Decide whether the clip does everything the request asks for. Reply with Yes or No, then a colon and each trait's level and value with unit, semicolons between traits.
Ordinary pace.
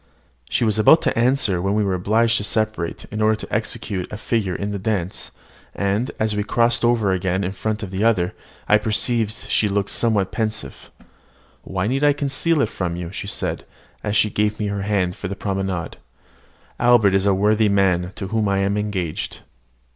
Yes: average, 195 wpm